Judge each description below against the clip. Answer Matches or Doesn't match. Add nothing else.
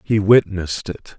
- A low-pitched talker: Matches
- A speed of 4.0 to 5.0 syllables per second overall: Matches